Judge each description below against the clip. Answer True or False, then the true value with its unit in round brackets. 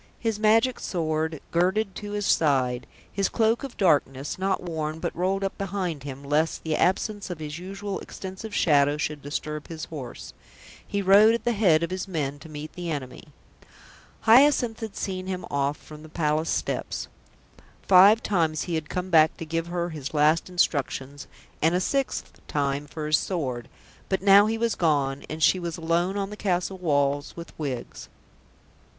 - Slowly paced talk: False (175 wpm)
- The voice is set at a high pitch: False (170 Hz)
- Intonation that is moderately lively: True (4.5 semitones)